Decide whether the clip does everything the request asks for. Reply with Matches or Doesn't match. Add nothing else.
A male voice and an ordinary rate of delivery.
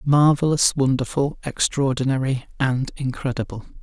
Doesn't match